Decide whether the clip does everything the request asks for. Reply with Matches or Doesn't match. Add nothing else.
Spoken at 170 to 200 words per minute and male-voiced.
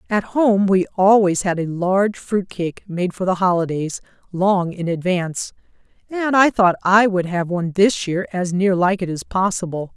Doesn't match